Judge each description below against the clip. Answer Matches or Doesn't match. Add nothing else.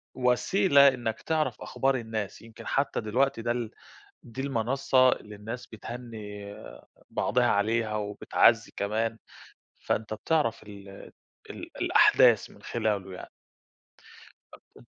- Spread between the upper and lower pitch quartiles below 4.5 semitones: Matches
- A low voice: Matches